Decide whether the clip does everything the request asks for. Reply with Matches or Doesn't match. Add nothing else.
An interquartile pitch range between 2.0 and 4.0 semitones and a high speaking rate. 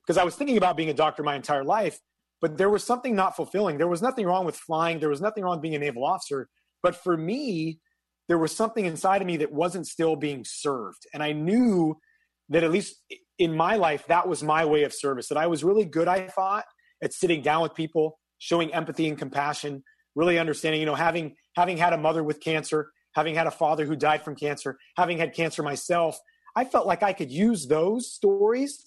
Matches